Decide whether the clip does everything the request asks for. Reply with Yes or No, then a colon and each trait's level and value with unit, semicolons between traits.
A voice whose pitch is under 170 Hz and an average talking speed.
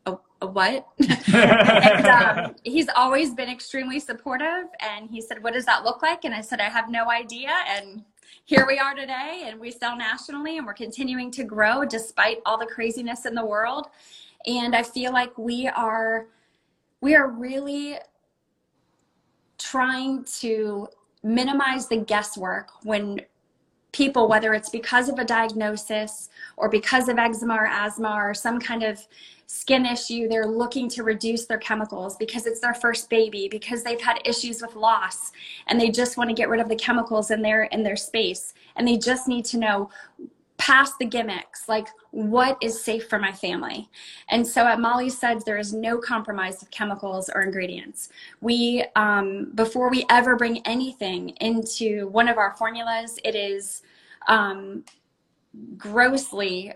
No: high, 230 Hz; average, 165 wpm